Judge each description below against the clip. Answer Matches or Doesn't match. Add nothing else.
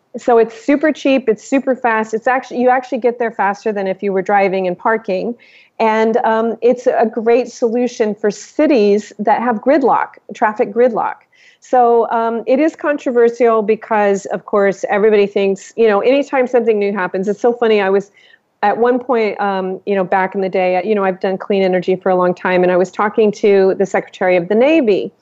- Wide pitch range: Doesn't match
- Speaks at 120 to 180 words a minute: Doesn't match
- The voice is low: Doesn't match